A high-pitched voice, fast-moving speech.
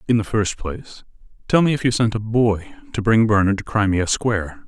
No: low, 110 Hz; fast, 220 wpm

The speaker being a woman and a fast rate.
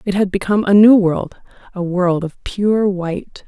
No: female; average, 190 wpm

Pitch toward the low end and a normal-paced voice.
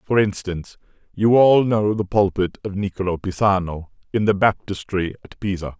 Yes: low, 100 Hz; average, 155 wpm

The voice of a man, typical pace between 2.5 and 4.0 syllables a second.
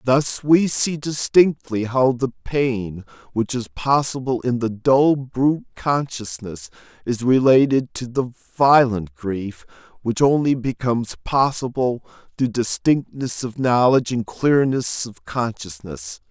Yes: male; 3.8 syllables/s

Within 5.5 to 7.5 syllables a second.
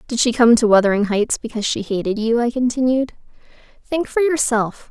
Yes: 5.7 syllables/s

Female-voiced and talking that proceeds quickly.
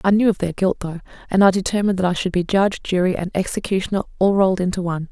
Yes: female; fast, 245 wpm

